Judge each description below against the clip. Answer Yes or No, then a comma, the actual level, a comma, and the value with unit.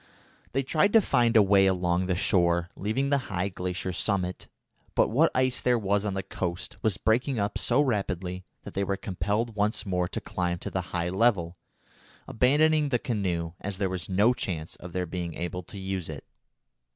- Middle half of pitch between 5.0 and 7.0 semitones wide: No, average, 4.4 semitones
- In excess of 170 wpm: Yes, average, 190 wpm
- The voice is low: Yes, very low, 95 Hz